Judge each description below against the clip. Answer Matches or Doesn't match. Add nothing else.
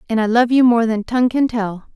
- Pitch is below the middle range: Doesn't match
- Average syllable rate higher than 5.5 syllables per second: Matches